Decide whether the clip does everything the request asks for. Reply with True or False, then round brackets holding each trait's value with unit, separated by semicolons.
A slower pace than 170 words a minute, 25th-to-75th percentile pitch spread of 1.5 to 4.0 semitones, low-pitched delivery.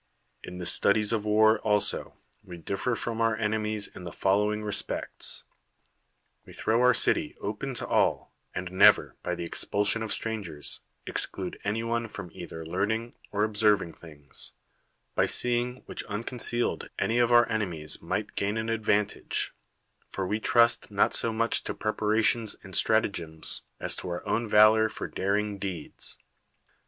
True (155 wpm; 2.8 semitones; 105 Hz)